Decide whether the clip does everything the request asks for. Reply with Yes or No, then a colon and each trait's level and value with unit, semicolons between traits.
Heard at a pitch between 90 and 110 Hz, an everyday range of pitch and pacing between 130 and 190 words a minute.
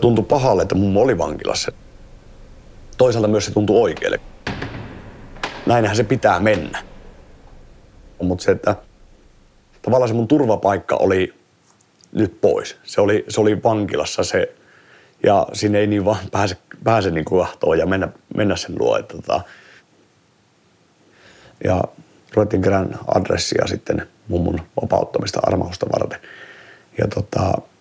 No: low, 105 Hz; average, 3.1 semitones; average, 120 wpm